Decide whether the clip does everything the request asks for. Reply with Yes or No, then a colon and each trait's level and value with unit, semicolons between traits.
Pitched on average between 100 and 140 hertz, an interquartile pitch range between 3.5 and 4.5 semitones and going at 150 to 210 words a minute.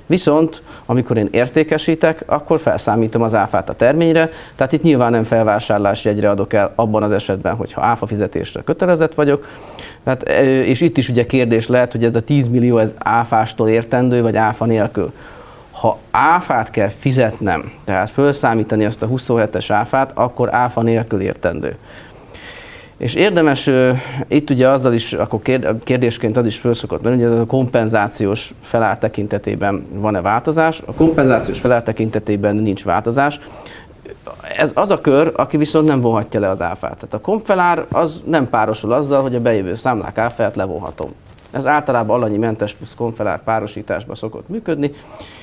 Yes: low, 120 Hz; average, 4.2 semitones; fast, 155 wpm